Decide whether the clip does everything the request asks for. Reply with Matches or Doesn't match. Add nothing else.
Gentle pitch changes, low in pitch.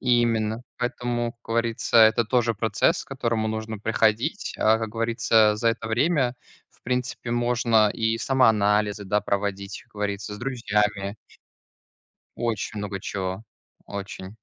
Matches